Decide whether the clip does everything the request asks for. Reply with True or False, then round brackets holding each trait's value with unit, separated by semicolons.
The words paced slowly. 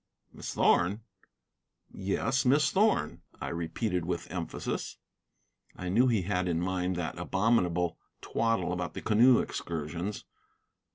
True (120 wpm)